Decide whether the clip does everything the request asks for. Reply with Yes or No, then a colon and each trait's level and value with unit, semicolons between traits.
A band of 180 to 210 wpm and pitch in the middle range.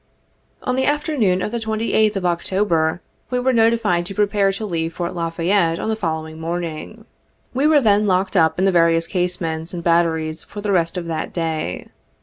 Yes: average, 195 wpm; medium, 180 Hz